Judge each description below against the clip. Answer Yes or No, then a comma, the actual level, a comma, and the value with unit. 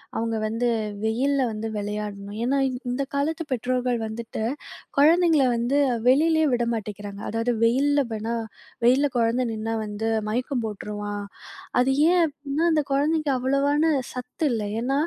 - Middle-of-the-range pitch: No, high, 245 Hz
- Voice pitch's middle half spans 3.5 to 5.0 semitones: Yes, average, 4.2 semitones